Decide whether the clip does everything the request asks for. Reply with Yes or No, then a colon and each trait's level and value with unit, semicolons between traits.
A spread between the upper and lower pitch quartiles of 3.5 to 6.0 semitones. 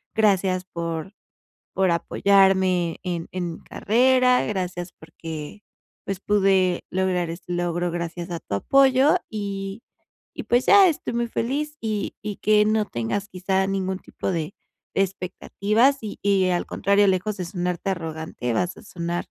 No: average, 3.1 semitones